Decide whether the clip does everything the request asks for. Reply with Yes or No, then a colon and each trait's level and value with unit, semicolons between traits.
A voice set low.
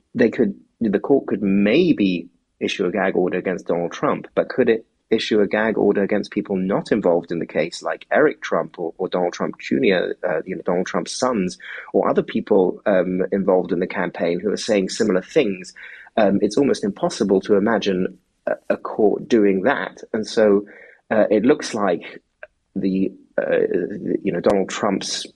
Yes: low, 105 Hz